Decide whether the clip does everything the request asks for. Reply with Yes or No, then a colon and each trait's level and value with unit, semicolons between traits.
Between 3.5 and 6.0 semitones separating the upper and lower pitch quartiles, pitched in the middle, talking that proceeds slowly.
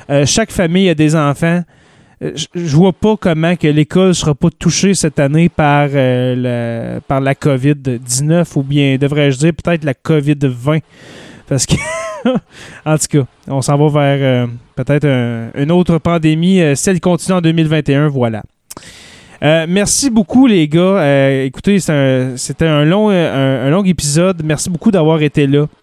No: average, 3.8 semitones; medium, 150 Hz; average, 175 wpm